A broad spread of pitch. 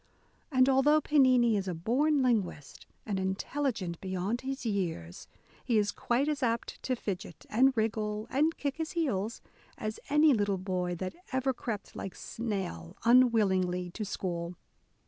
Yes: wide, 5.7 semitones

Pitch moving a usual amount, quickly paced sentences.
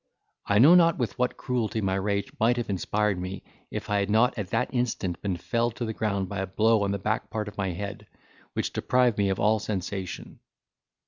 Yes: average, 3.0 semitones; fast, 215 wpm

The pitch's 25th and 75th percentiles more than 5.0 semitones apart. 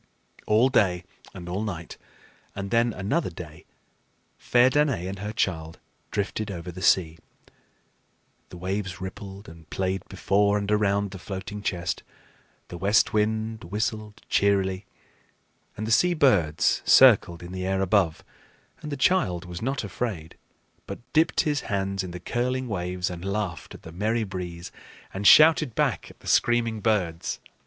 No: average, 3.6 semitones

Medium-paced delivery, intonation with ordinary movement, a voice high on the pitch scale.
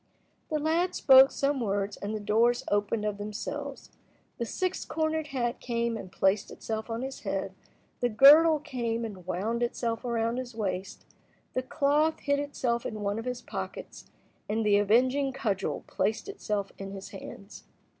Yes: average, 165 wpm; average, 4.7 semitones; high, 235 Hz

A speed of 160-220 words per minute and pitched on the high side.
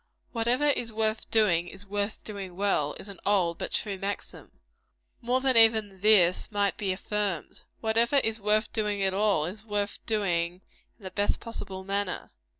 Yes: average, 165 wpm; high, 205 Hz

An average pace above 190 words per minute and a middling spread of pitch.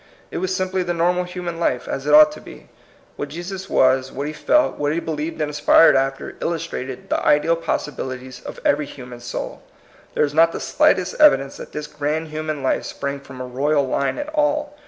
Yes: average, 200 wpm; average, 4.0 semitones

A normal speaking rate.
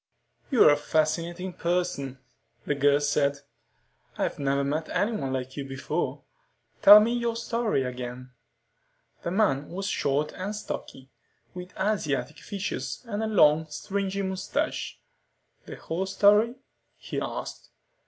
No: slow, 125 wpm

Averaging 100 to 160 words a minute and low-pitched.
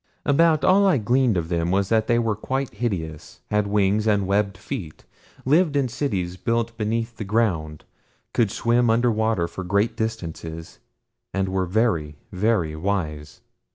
Yes: average, 155 wpm; low, 105 Hz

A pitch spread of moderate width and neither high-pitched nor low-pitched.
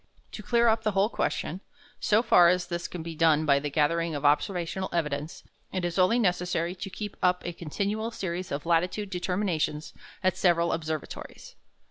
Yes: average, 3.1 semitones; medium, 175 Hz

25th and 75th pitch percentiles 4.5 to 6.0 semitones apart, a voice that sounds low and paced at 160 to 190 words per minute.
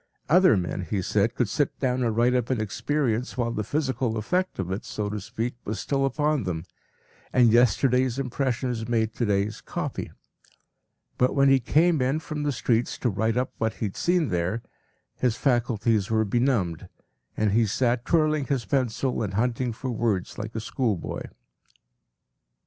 No: average, 3.5 semitones; low, 120 Hz; average, 170 wpm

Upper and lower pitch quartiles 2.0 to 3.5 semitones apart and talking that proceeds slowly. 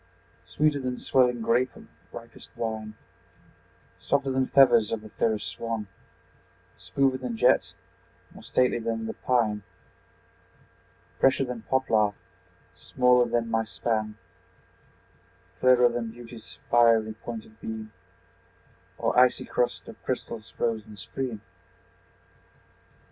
Yes: narrow, 2.4 semitones; slow, 110 wpm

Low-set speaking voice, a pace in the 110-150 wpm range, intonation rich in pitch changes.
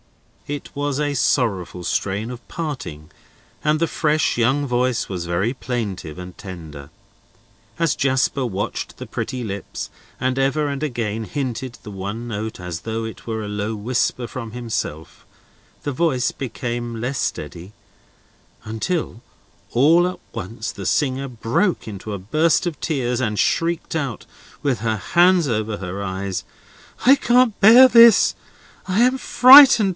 Yes: low, 120 Hz; average, 145 wpm; wide, 5.9 semitones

